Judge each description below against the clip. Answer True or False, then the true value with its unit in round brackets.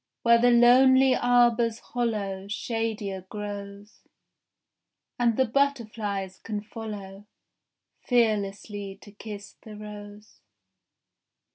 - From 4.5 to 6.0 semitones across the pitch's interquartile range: False (2.7 semitones)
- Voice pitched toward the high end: True (215 Hz)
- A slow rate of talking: True (90 wpm)